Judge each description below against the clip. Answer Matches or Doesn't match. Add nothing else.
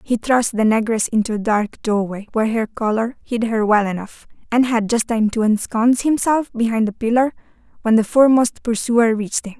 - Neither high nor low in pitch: Doesn't match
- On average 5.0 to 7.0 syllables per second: Matches